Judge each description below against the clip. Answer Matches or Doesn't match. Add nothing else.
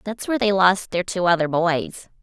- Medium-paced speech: Doesn't match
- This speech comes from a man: Doesn't match